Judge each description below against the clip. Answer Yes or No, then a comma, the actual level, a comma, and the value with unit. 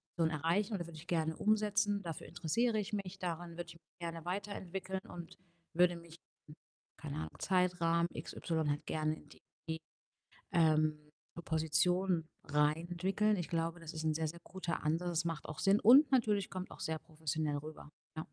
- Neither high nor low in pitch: Yes, medium, 170 Hz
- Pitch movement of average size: Yes, average, 3.0 semitones